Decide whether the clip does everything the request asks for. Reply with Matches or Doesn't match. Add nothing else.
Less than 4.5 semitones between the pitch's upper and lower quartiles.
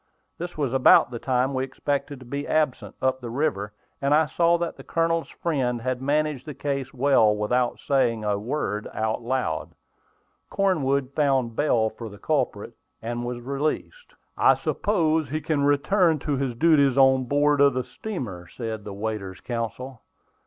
Matches